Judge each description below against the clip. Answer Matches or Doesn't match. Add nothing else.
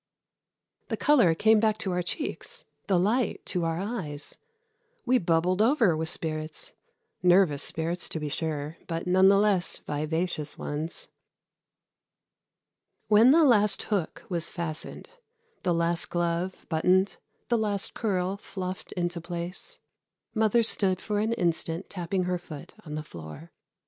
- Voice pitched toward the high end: Doesn't match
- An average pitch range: Matches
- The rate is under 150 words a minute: Matches